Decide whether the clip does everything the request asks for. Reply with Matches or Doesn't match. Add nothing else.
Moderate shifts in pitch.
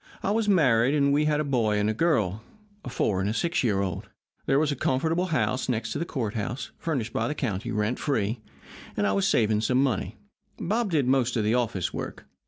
Doesn't match